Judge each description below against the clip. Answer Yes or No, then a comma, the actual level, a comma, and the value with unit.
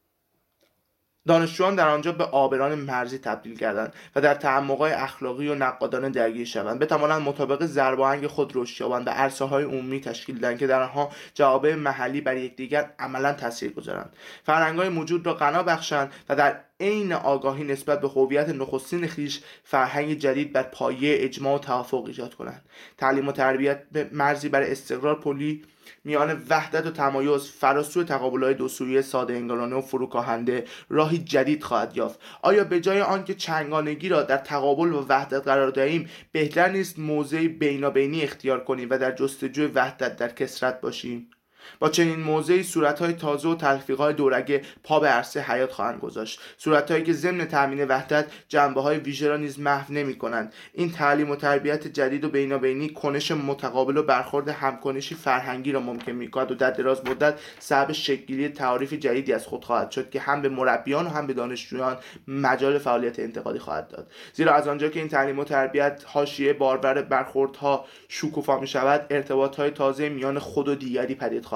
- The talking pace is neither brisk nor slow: No, fast, 175 wpm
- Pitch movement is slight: Yes, narrow, 2.2 semitones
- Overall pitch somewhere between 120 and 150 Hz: Yes, medium, 140 Hz